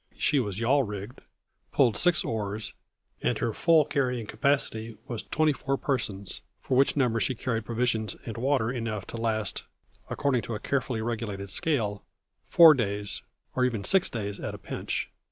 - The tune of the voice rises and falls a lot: No, average, 4.0 semitones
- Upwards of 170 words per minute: No, average, 165 wpm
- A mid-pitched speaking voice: No, low, 115 Hz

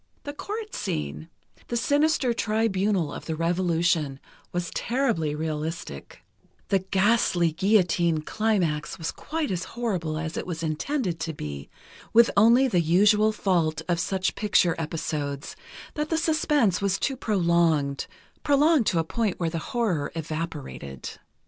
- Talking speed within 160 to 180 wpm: No, slow, 135 wpm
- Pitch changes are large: Yes, wide, 5.8 semitones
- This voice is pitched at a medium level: Yes, medium, 175 Hz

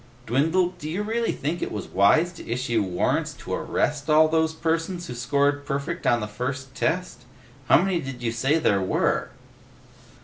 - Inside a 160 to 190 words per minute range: Yes, average, 175 wpm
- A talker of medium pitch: Yes, medium, 145 Hz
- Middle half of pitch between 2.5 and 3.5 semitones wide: No, average, 5.2 semitones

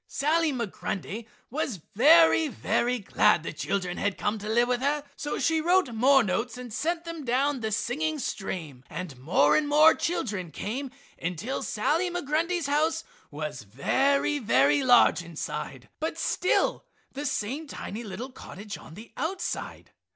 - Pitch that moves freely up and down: Yes, wide, 7.0 semitones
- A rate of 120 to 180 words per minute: Yes, average, 150 wpm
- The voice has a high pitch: Yes, very high, 250 Hz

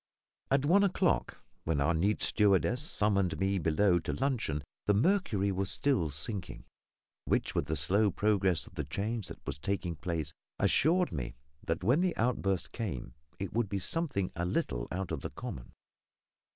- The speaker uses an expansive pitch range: Yes, wide, 5.9 semitones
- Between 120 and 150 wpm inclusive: No, average, 165 wpm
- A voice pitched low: Yes, very low, 95 Hz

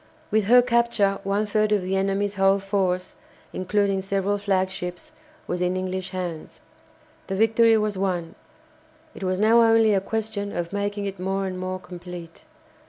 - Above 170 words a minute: No, average, 160 wpm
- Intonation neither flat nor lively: No, narrow, 2.2 semitones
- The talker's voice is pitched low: No, high, 195 Hz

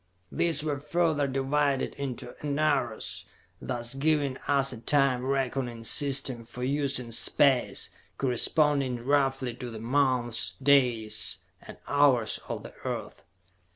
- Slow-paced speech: Yes, slow, 120 wpm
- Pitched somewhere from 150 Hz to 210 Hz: No, low, 135 Hz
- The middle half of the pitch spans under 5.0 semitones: Yes, average, 2.7 semitones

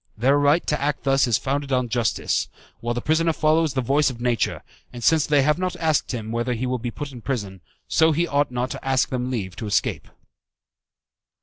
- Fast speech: Yes, fast, 215 wpm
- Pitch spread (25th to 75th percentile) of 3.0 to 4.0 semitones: Yes, average, 3.5 semitones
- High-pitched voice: No, low, 130 Hz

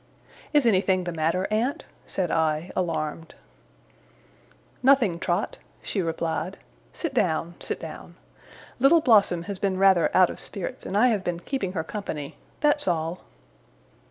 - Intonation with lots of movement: No, average, 4.5 semitones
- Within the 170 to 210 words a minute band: No, average, 140 wpm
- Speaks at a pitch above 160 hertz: Yes, medium, 185 Hz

